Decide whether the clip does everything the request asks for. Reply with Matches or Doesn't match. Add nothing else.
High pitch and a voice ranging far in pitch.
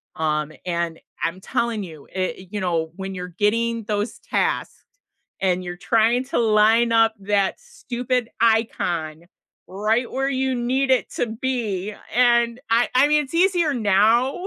Doesn't match